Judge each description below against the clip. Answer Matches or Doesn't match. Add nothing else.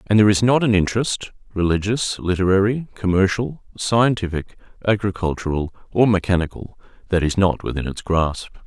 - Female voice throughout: Doesn't match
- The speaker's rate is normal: Doesn't match